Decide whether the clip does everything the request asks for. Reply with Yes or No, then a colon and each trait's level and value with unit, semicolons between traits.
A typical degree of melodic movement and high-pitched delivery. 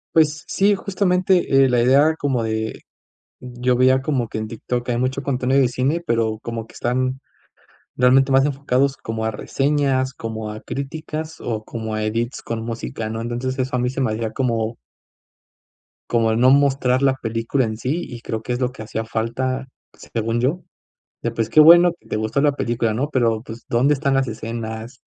No: average, 3.1 semitones; low, 125 Hz